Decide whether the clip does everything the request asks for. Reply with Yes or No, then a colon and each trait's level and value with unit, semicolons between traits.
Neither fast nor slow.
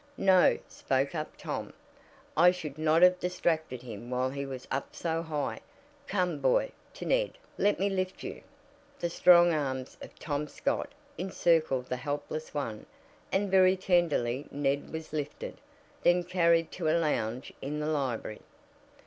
Yes: average, 150 wpm